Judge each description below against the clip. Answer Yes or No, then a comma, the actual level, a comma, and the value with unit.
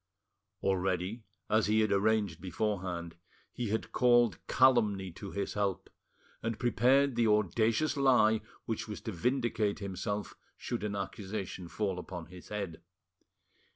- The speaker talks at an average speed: No, slow, 130 wpm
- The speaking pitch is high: No, low, 105 Hz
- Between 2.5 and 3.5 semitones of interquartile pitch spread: Yes, average, 3.2 semitones